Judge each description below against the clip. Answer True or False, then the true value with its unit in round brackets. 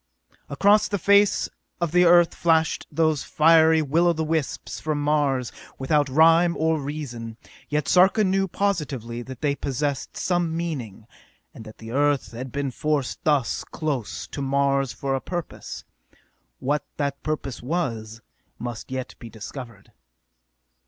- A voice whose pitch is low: False (145 Hz)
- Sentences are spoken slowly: False (145 wpm)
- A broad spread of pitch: False (4.0 semitones)